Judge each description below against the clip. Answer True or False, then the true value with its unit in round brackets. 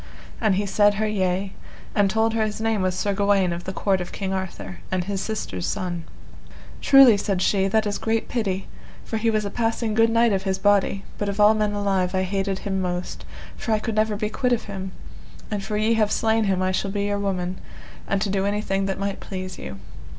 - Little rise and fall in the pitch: True (2.2 semitones)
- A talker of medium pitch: False (200 Hz)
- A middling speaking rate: False (225 wpm)